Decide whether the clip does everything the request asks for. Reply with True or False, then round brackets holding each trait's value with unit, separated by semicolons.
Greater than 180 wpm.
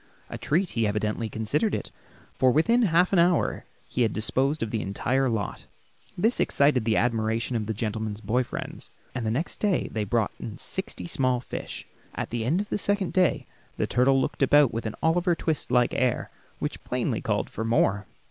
True (195 wpm)